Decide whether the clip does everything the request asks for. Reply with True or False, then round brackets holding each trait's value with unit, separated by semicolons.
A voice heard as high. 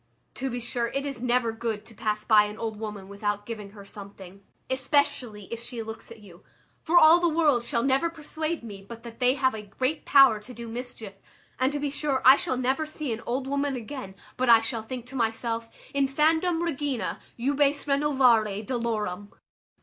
True (245 Hz)